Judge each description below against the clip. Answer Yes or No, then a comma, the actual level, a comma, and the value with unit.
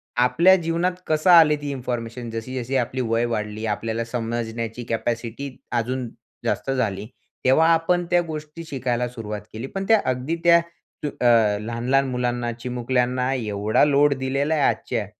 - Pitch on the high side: No, low, 125 Hz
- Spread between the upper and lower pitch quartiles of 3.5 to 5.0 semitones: Yes, average, 3.9 semitones